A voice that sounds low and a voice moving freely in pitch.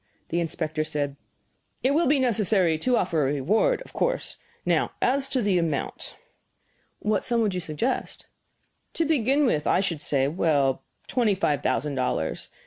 No: medium, 185 Hz; wide, 8.8 semitones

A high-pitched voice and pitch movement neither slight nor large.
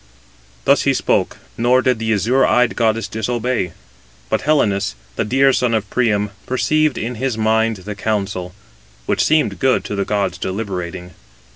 No: low, 110 Hz; average, 4.0 semitones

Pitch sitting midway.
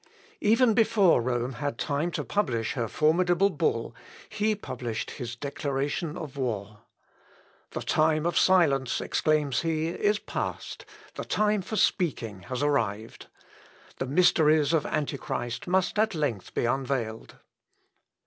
Yes: medium, 150 Hz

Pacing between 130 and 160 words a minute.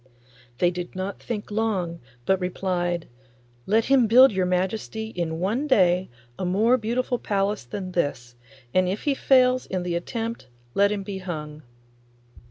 Yes: average, 155 wpm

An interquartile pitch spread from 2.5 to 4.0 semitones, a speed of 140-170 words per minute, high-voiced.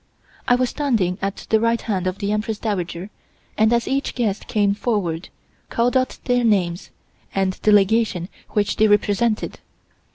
Yes: average, 3.2 semitones; average, 160 wpm; high, 210 Hz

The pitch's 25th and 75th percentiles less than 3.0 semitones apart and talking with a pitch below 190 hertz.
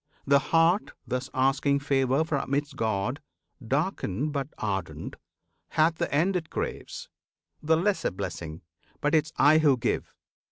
No: average, 3.6 semitones; medium, 140 Hz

